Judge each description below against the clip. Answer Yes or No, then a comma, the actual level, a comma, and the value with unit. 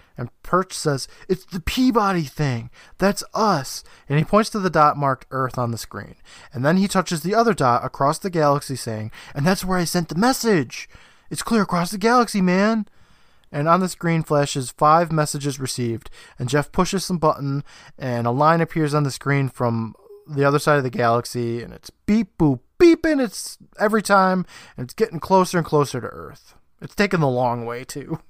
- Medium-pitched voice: Yes, medium, 155 Hz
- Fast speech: No, average, 195 wpm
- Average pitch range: No, wide, 6.2 semitones